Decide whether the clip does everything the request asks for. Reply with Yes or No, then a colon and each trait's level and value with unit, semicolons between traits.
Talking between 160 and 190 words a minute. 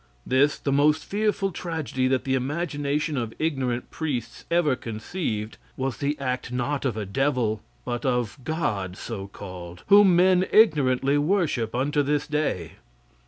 No: average, 145 wpm